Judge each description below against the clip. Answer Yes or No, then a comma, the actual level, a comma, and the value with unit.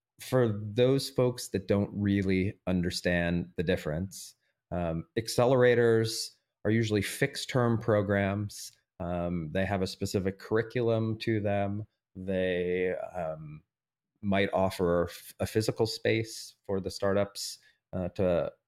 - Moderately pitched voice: No, low, 100 Hz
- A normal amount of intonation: Yes, average, 3.4 semitones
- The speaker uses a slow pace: Yes, slow, 115 wpm